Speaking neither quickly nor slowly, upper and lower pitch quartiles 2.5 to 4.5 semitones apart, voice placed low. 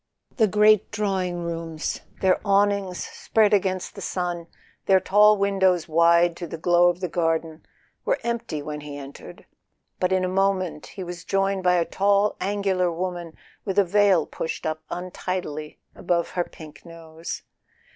No: average, 160 wpm; average, 2.8 semitones; medium, 180 Hz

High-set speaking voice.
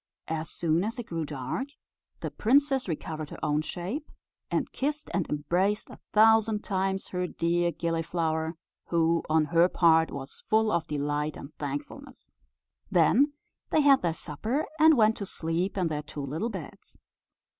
No: medium, 170 Hz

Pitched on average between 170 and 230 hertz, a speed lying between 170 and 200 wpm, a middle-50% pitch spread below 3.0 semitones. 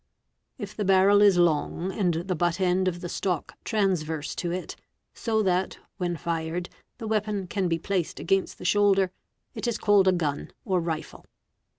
Yes: medium, 185 Hz; average, 175 wpm; narrow, 2.6 semitones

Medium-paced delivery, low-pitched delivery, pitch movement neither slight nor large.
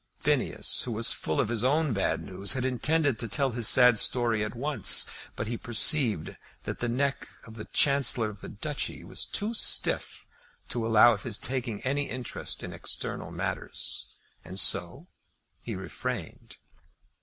Yes: average, 165 wpm; low, 120 Hz; average, 3.7 semitones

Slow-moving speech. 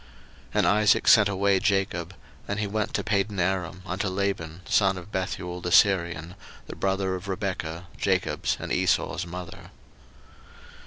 No: average, 145 wpm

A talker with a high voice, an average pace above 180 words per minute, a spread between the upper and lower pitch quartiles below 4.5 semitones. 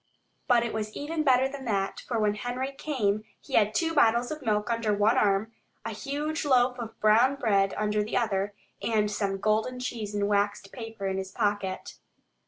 Yes: high, 220 Hz; average, 190 wpm; average, 3.5 semitones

